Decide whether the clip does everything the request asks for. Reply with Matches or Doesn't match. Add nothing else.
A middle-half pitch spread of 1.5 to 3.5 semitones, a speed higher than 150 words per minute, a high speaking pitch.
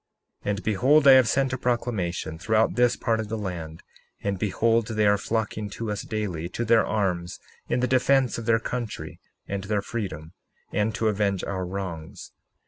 Doesn't match